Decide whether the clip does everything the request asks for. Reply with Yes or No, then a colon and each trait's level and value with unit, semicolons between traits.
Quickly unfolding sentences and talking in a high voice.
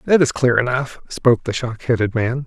No: fast, 220 wpm; low, 125 Hz